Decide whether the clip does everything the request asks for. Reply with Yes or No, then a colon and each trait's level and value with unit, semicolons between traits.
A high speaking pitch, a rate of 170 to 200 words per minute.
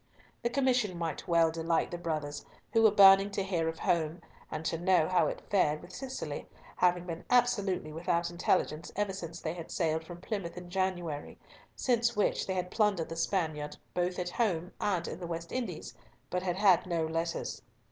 No: medium, 175 Hz; average, 190 wpm